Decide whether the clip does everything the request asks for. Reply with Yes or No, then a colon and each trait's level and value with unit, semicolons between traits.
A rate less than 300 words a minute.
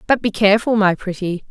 Yes: average, 200 wpm